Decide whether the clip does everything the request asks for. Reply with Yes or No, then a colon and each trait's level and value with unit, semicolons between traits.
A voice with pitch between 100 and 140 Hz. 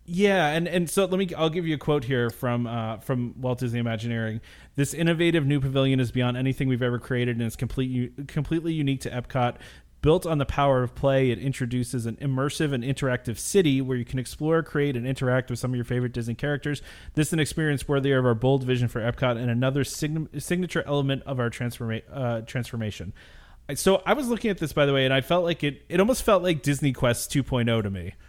Yes: low, 135 Hz